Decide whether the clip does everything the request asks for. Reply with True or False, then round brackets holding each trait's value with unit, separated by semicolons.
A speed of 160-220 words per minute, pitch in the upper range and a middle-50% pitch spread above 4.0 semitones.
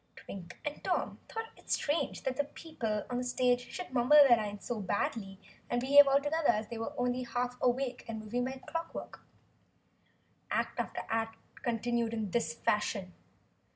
False (175 wpm; 245 Hz; 3.2 semitones)